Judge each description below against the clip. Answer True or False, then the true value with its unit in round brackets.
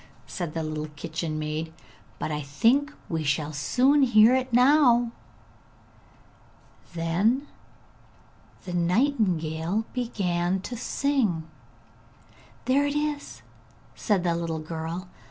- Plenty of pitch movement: True (7.7 semitones)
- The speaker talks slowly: True (105 wpm)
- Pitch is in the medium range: True (180 Hz)